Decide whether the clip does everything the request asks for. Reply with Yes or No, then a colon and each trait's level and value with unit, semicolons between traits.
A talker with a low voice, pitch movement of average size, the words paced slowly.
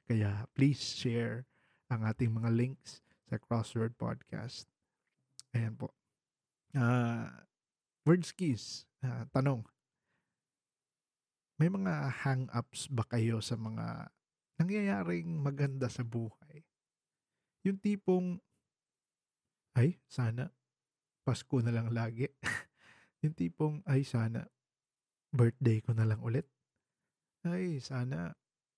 Yes: low, 130 Hz; average, 4.4 semitones; slow, 100 wpm